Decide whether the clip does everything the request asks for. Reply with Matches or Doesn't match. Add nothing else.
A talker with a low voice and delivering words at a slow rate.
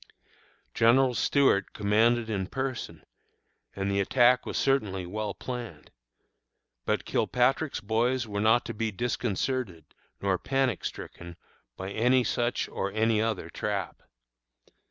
Matches